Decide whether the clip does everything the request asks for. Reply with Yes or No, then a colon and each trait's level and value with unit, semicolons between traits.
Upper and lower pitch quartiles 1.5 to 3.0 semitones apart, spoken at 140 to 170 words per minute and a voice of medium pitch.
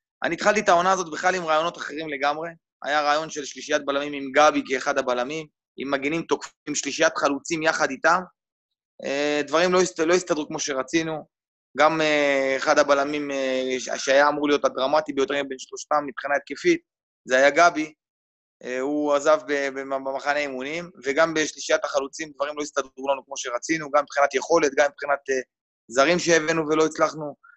Yes: narrow, 2.5 semitones; fast, 150 wpm; medium, 145 Hz